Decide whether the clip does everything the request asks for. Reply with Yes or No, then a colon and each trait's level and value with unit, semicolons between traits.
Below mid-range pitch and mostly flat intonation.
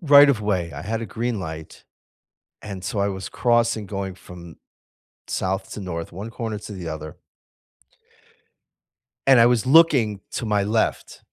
No: low, 105 Hz; average, 3.5 semitones